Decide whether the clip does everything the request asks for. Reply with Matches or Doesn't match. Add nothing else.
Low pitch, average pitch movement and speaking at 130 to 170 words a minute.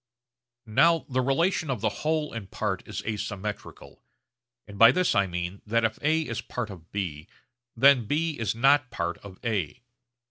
Doesn't match